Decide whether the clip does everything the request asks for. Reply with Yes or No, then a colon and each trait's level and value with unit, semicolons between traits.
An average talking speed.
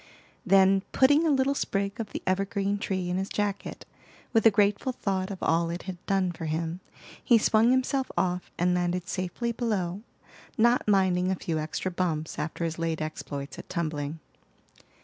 Yes: average, 170 wpm